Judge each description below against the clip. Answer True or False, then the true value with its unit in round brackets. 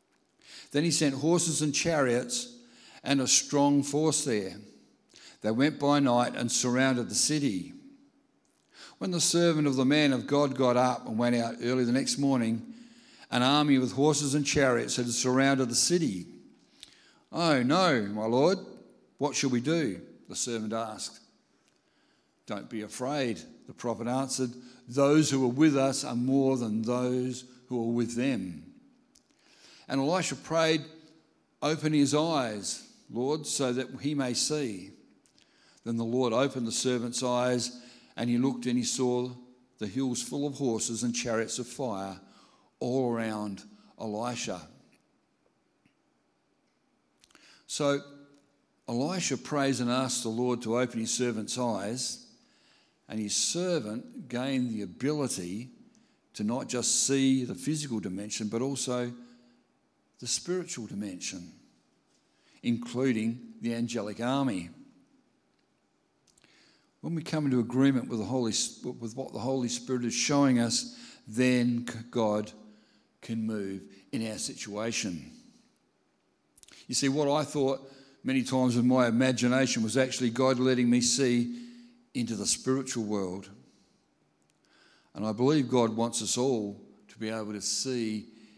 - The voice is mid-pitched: False (125 Hz)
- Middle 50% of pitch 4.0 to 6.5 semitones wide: False (3.3 semitones)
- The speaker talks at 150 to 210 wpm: False (140 wpm)